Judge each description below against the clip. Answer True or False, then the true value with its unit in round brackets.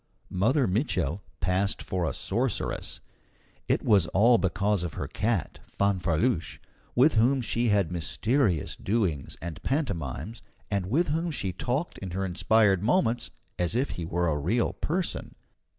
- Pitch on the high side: False (100 Hz)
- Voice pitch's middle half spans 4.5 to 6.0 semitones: True (5.5 semitones)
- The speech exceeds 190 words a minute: False (145 wpm)